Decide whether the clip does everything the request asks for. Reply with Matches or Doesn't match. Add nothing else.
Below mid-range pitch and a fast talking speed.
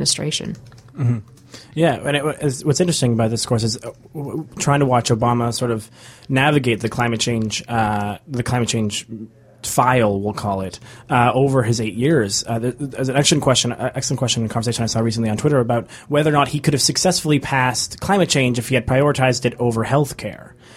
Matches